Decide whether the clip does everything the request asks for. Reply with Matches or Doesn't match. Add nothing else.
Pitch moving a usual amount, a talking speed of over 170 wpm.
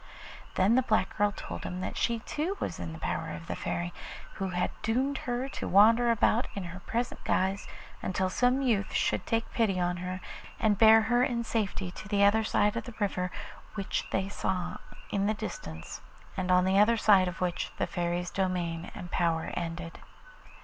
Matches